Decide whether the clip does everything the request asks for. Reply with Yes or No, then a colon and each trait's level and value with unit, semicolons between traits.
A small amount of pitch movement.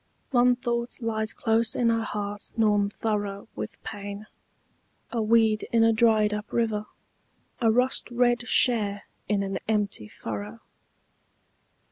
Yes: narrow, 2.1 semitones